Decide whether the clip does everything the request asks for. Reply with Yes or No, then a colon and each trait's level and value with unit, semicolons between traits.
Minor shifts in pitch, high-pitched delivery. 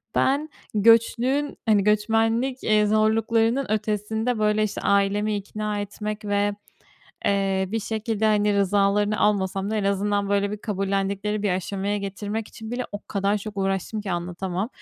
Yes: narrow, 1.6 semitones; high, 210 Hz